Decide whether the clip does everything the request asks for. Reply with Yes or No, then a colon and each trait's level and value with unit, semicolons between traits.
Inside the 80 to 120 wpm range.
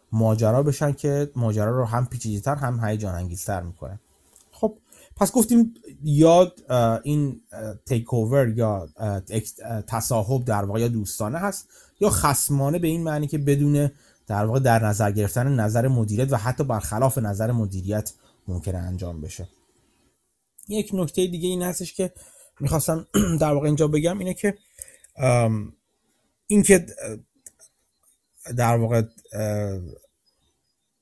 No: average, 130 wpm